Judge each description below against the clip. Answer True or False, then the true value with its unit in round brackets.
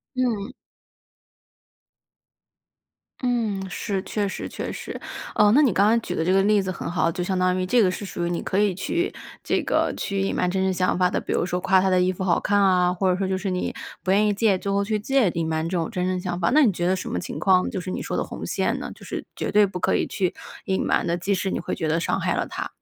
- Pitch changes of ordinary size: False (2.0 semitones)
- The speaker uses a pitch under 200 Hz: True (190 Hz)